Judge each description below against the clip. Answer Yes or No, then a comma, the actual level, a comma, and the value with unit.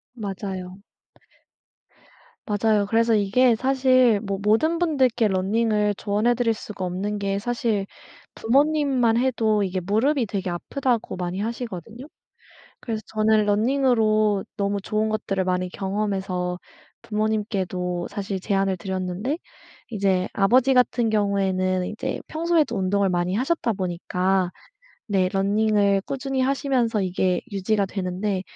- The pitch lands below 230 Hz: Yes, high, 210 Hz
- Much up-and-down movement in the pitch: No, average, 3.6 semitones